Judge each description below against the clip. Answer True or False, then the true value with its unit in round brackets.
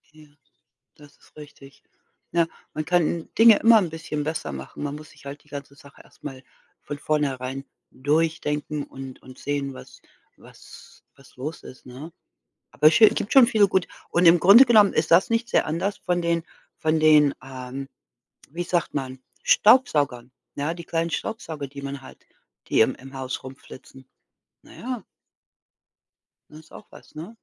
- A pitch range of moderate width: True (3.8 semitones)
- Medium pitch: True (150 Hz)